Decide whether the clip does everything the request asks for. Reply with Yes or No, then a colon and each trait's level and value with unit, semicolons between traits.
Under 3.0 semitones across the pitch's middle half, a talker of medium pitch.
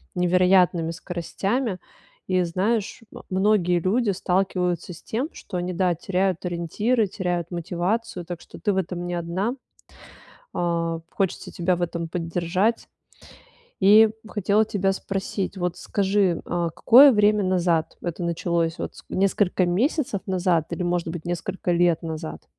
Yes: narrow, 2.4 semitones; medium, 180 Hz